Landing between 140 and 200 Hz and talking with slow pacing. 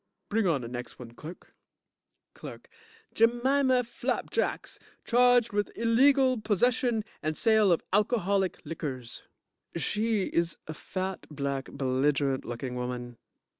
Yes: high, 190 Hz; slow, 125 wpm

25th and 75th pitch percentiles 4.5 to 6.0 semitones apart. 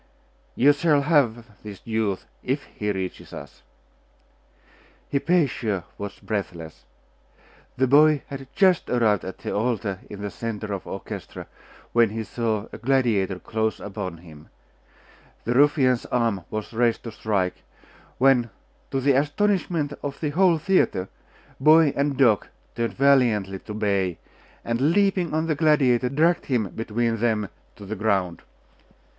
Yes: wide, 5.5 semitones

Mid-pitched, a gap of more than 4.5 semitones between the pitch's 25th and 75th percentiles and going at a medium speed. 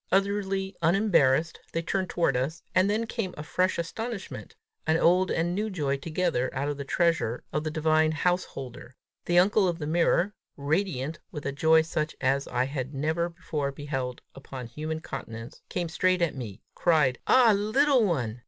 Yes: medium, 160 Hz; average, 5.0 semitones; average, 175 wpm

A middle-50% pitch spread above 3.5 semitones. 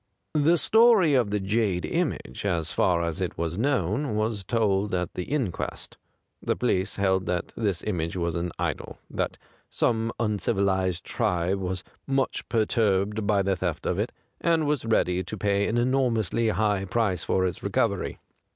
Yes: average, 4.0 semitones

